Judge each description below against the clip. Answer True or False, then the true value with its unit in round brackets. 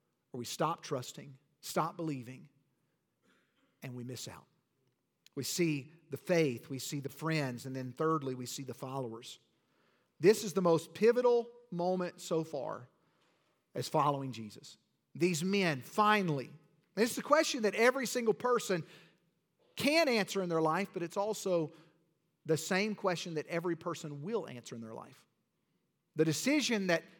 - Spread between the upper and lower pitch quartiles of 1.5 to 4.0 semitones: False (5.2 semitones)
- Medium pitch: True (165 Hz)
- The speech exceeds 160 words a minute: False (150 wpm)